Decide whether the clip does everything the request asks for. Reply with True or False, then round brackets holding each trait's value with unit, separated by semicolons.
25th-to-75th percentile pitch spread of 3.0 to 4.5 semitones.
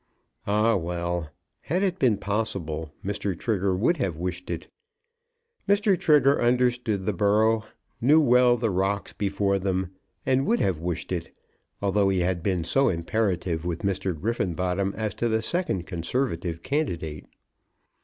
False (5.2 semitones)